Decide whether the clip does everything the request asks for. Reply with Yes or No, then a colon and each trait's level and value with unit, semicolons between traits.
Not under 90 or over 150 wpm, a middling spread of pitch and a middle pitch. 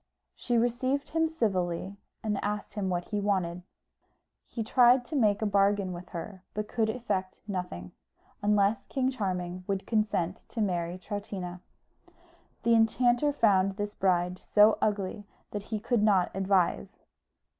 No: average, 145 wpm; average, 3.3 semitones; high, 205 Hz